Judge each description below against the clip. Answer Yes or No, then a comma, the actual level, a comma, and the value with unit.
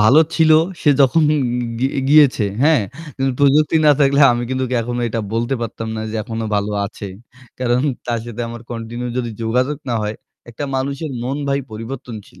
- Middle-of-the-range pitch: No, low, 125 Hz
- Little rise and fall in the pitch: No, average, 3.3 semitones